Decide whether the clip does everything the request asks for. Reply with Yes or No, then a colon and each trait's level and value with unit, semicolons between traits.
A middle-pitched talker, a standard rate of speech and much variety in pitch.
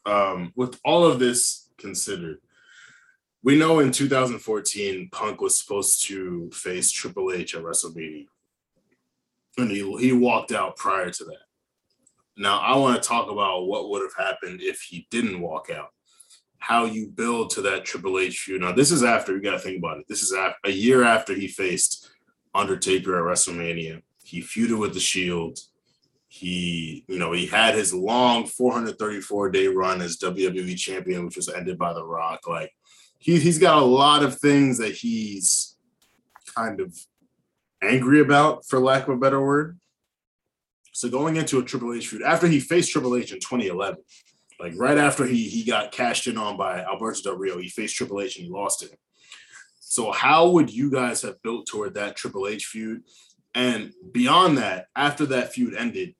No: low, 125 Hz; average, 180 wpm; wide, 8.2 semitones